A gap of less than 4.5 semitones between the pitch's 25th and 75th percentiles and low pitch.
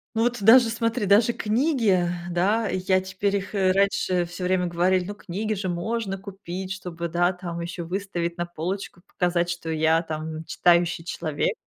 No: average, 2.7 semitones; medium, 185 Hz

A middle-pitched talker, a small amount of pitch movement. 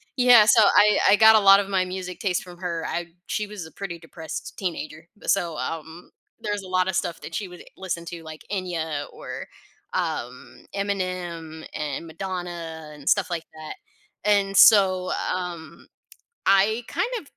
No: medium, 180 Hz; average, 3.2 semitones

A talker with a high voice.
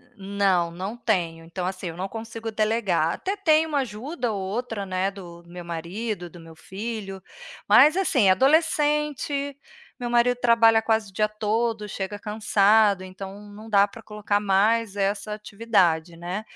Yes: high, 210 Hz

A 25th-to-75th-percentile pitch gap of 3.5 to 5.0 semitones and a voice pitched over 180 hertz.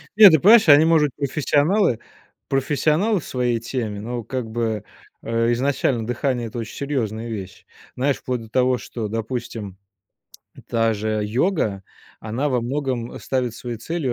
No: average, 4.0 semitones; low, 125 Hz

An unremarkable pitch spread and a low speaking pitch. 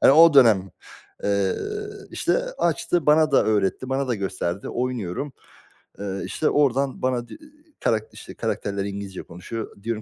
No: wide, 5.8 semitones; low, 115 Hz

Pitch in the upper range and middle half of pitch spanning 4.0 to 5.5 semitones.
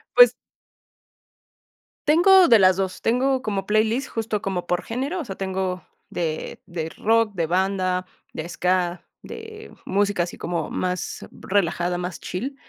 Yes: high, 195 Hz; average, 4.3 semitones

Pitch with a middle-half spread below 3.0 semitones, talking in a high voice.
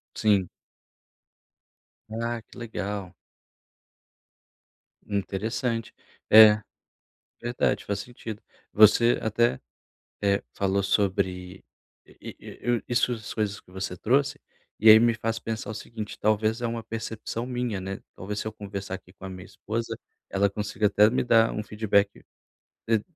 No: narrow, 2.4 semitones; low, 110 Hz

